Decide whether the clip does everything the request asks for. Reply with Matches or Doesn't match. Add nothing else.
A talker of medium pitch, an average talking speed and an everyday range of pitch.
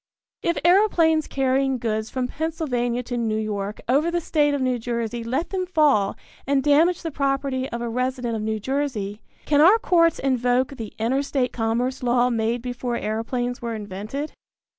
Doesn't match